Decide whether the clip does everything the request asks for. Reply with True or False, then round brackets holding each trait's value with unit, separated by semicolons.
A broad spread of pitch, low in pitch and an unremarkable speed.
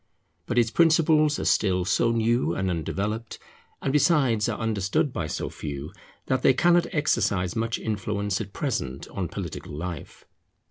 True (6.3 semitones; 110 Hz; 150 wpm)